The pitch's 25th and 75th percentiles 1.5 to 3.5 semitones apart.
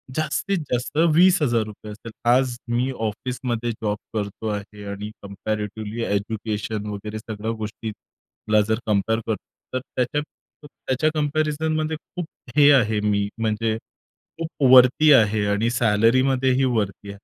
No: average, 3.9 semitones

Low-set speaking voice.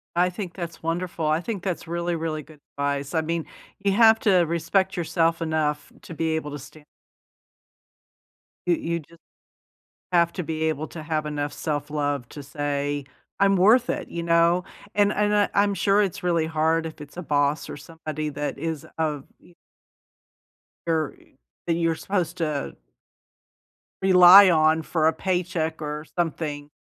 No: medium, 165 Hz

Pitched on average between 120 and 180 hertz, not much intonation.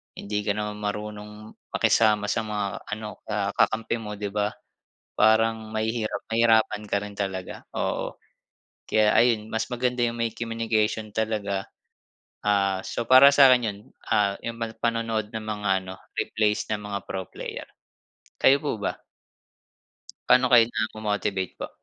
No: low, 110 Hz; narrow, 1.7 semitones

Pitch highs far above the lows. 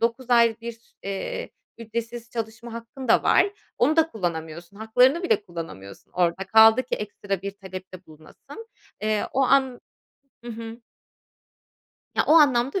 No: average, 4.1 semitones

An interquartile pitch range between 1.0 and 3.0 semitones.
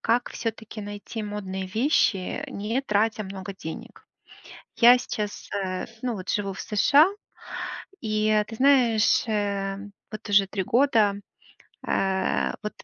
Yes: narrow, 2.4 semitones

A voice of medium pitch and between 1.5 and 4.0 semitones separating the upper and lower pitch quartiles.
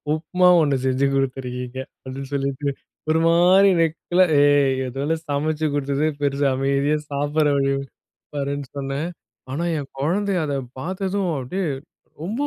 Yes: medium, 145 Hz; average, 3.2 semitones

